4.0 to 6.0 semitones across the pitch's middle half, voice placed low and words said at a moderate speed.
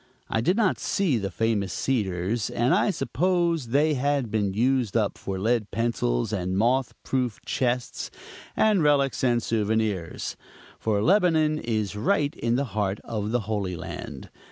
Yes: average, 5.3 semitones; low, 115 Hz; average, 155 wpm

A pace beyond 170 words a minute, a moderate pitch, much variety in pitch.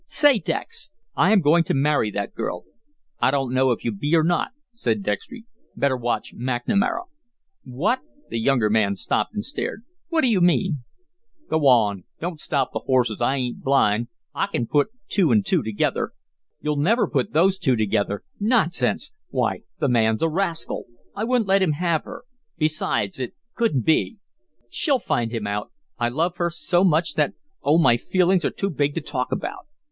Yes: average, 180 wpm; medium, 150 Hz; wide, 7.6 semitones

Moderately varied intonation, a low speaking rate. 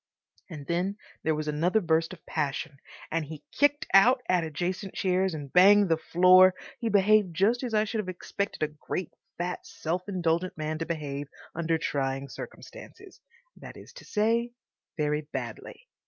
No: average, 4.5 semitones; average, 160 wpm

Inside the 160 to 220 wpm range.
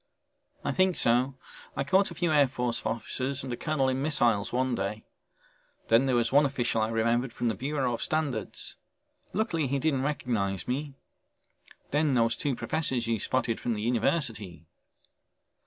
Yes: average, 165 wpm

